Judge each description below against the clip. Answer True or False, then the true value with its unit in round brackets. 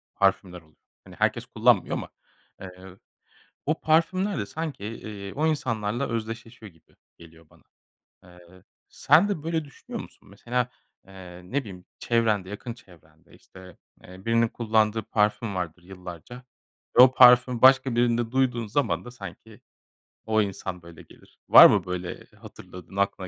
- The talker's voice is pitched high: False (110 Hz)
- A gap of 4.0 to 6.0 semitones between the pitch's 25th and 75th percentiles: True (5.1 semitones)